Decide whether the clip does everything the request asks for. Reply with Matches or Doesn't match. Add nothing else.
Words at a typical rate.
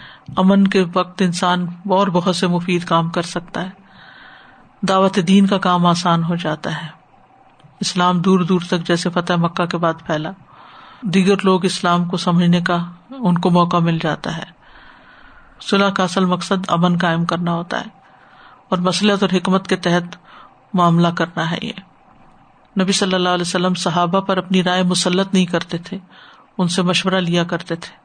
Matches